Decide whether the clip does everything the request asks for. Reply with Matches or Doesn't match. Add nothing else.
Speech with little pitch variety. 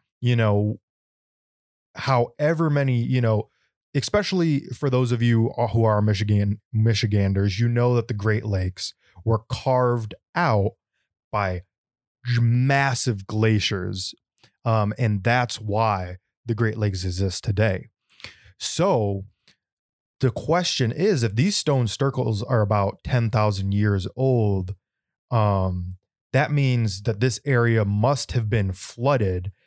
Doesn't match